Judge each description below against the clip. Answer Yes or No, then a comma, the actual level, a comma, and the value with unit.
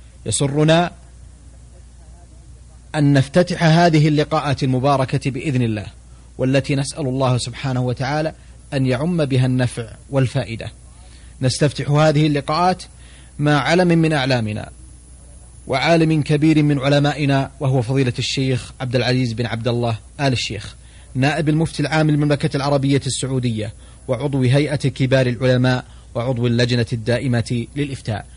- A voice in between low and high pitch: No, low, 130 Hz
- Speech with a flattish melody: No, average, 4.0 semitones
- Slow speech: No, average, 110 wpm